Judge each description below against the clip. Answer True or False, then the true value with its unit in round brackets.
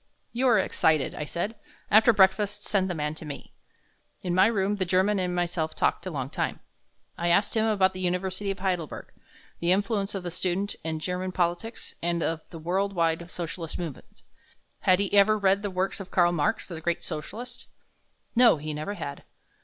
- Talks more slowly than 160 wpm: False (190 wpm)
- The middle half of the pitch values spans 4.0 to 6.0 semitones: False (2.9 semitones)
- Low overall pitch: False (185 Hz)